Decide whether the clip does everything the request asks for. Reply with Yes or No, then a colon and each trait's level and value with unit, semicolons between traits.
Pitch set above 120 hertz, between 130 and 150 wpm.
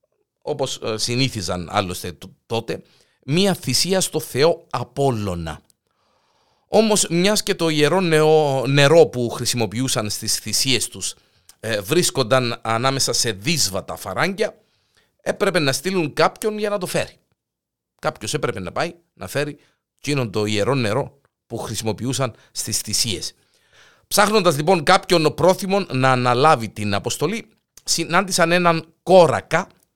No: medium, 140 Hz; average, 120 wpm